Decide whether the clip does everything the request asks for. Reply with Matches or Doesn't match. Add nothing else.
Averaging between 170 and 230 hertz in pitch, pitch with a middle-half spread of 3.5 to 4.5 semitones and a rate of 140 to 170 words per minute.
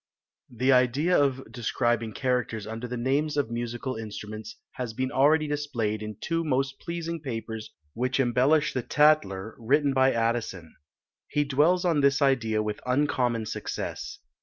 Doesn't match